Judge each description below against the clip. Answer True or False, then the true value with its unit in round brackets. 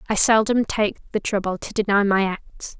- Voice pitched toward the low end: False (205 Hz)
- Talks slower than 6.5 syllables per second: True (4.9 syllables/s)